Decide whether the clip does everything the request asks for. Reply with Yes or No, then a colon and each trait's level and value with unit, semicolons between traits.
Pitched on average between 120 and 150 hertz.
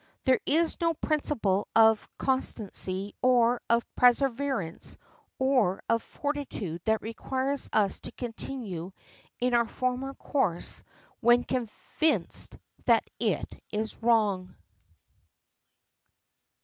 No: high, 235 Hz